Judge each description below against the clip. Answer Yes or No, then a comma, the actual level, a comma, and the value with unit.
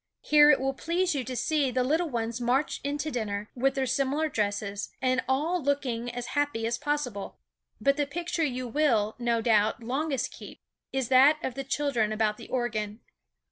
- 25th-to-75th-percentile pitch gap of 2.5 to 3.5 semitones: No, average, 4.0 semitones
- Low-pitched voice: No, very high, 260 Hz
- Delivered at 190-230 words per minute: No, average, 180 wpm